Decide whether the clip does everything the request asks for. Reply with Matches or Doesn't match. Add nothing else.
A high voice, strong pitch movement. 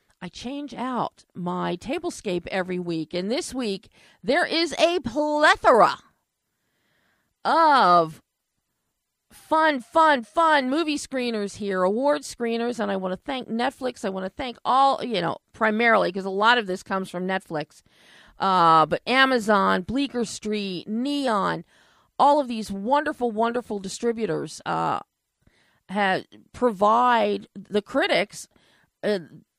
Matches